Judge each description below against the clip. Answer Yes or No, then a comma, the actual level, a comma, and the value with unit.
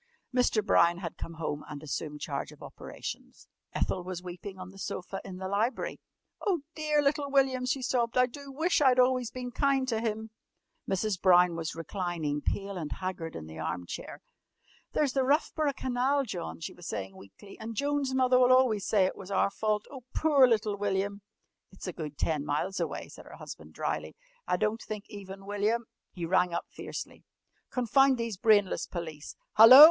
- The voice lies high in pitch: Yes, high, 205 Hz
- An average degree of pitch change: No, wide, 6.1 semitones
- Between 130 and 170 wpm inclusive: No, average, 185 wpm